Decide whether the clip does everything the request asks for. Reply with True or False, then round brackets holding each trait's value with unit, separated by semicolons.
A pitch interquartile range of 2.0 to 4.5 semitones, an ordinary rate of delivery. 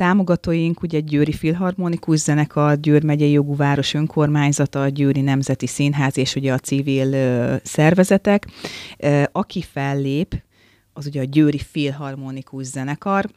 True (2.5 semitones; 130 wpm)